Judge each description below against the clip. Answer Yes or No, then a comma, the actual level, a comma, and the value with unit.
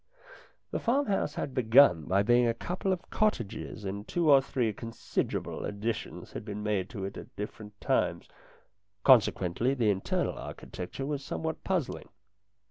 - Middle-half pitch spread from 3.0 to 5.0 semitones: No, wide, 5.5 semitones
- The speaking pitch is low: Yes, low, 115 Hz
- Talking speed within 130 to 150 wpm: Yes, average, 145 wpm